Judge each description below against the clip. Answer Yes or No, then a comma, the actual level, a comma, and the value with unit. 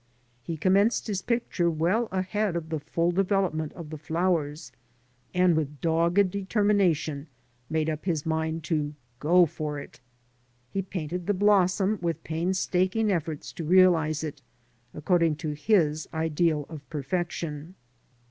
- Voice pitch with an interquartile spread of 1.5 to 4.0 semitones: Yes, average, 3.1 semitones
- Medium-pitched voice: Yes, medium, 170 Hz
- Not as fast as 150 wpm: Yes, slow, 135 wpm